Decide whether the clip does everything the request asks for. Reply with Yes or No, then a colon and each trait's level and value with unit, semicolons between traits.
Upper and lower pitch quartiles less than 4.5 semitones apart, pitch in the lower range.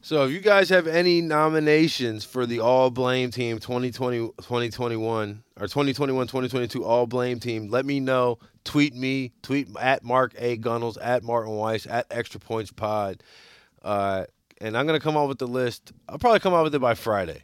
Yes: average, 3.3 semitones; low, 125 Hz